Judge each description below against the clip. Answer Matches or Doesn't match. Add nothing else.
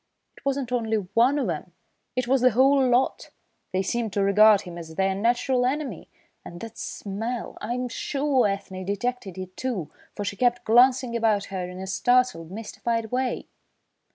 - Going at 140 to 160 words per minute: Doesn't match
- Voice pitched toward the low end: Doesn't match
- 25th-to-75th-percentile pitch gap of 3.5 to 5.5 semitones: Matches